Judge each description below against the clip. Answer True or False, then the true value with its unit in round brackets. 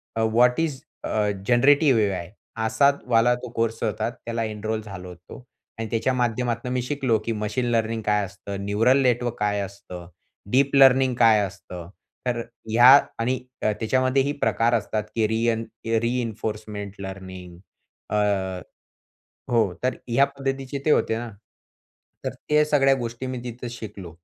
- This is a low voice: True (115 Hz)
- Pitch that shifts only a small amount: False (3.3 semitones)